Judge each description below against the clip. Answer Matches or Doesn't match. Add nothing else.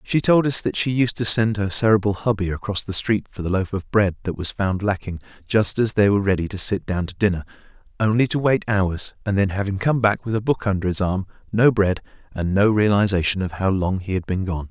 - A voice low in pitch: Matches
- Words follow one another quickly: Matches